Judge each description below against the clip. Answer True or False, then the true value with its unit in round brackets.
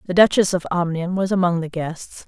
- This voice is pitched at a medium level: True (175 Hz)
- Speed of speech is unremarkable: False (210 wpm)